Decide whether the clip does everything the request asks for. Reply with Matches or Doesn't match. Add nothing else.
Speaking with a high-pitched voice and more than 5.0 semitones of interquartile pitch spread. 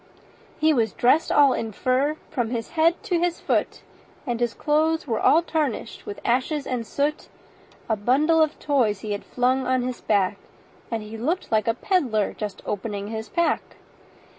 Matches